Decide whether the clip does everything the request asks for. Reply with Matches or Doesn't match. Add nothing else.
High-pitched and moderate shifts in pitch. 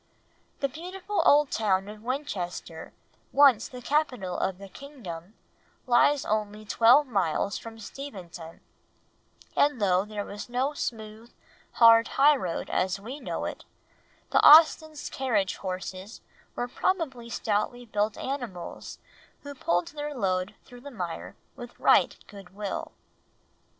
Doesn't match